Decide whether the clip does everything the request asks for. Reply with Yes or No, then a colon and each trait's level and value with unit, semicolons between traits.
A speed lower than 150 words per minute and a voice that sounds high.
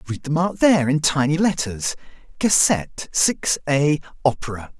No: average, 140 wpm; medium, 145 Hz